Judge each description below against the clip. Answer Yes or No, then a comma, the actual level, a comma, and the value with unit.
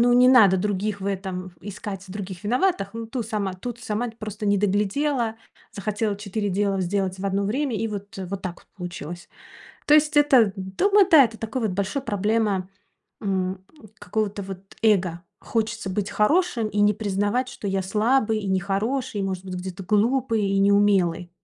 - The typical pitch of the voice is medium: No, high, 205 Hz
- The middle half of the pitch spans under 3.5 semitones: Yes, average, 2.8 semitones